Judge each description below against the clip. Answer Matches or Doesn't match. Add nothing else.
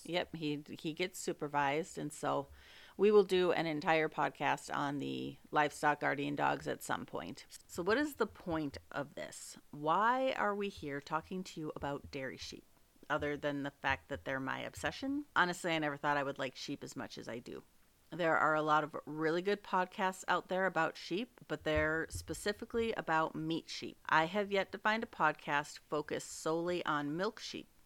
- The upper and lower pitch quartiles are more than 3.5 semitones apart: Matches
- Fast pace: Doesn't match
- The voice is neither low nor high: Matches